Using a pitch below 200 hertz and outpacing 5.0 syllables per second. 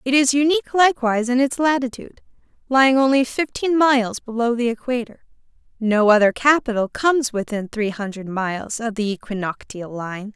No: high, 240 Hz; 5.5 syllables/s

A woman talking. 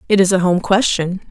Yes: female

